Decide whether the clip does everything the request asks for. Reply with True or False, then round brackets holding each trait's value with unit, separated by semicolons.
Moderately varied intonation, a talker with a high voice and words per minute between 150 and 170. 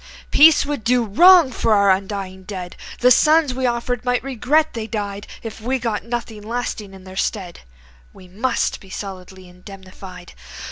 True (4.5 semitones; 220 Hz; 160 wpm)